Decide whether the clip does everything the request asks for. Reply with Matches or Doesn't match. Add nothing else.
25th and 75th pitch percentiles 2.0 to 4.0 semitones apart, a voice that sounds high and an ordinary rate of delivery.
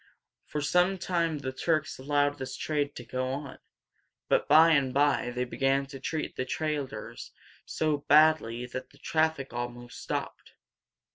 Doesn't match